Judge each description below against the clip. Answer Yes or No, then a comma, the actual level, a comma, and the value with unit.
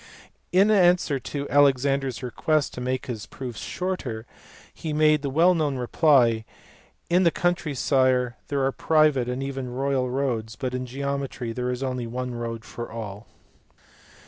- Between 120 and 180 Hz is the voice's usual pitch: Yes, low, 135 Hz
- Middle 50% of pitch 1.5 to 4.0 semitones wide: Yes, average, 2.9 semitones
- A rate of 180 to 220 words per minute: No, average, 165 wpm